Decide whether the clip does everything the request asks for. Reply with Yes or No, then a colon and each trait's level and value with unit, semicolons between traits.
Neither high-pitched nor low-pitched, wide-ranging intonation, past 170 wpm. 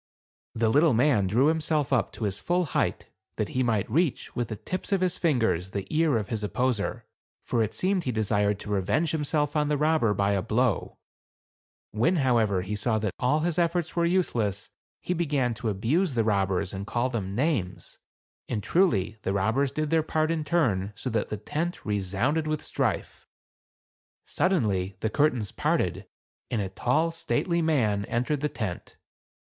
No: low, 125 Hz; wide, 7.1 semitones; average, 180 wpm